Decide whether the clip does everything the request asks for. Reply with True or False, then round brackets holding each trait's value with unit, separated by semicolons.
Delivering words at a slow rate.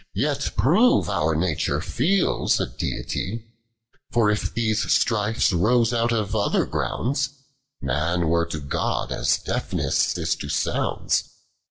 True (130 wpm)